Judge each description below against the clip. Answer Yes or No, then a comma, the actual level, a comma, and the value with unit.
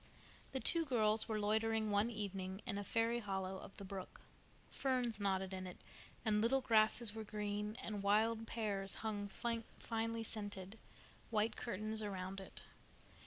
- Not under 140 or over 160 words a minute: Yes, average, 150 wpm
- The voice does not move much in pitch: Yes, narrow, 2.2 semitones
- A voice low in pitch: No, high, 215 Hz